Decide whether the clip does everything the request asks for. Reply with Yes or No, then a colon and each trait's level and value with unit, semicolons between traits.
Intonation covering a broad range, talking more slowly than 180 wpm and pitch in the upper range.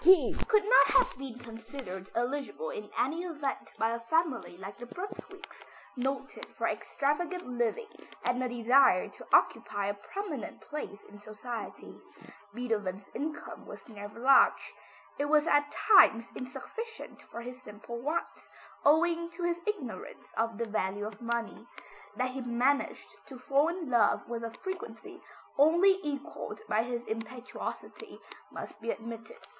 Yes: wide, 6.0 semitones; average, 145 wpm; very high, 255 Hz